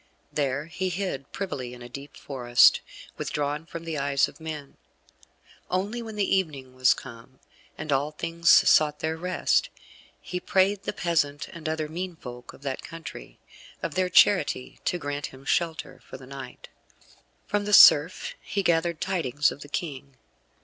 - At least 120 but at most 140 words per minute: No, average, 165 wpm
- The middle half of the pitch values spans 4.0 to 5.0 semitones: Yes, average, 4.3 semitones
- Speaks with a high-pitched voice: No, medium, 155 Hz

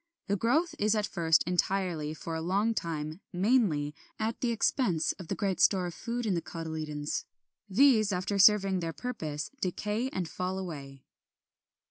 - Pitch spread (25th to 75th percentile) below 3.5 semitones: No, average, 4.8 semitones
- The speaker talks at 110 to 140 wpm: No, average, 160 wpm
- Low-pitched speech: No, medium, 185 Hz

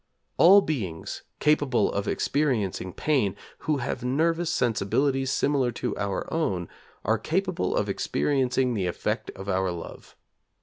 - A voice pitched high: No, low, 125 Hz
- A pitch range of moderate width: No, wide, 7.2 semitones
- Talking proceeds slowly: Yes, slow, 130 wpm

